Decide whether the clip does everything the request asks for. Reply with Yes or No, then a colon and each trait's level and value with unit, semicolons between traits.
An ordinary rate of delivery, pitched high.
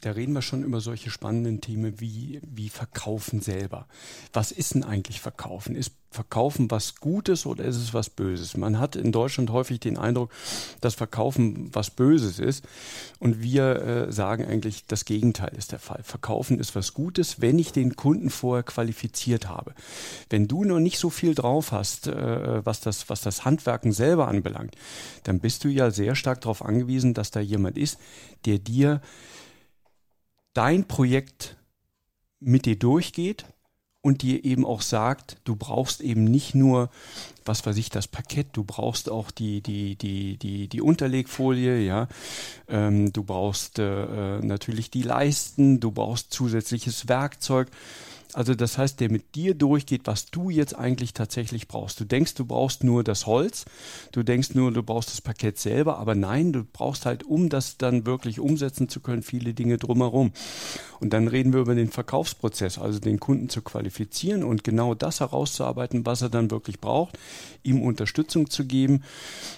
No: average, 170 wpm; low, 120 Hz